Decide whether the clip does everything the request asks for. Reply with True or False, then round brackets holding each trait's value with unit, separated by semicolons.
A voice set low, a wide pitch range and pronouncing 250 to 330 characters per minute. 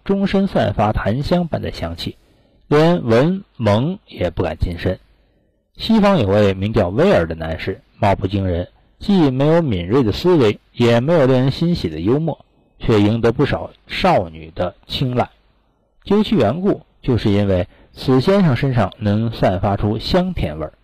False (115 Hz; 8.6 semitones; 235 characters per minute)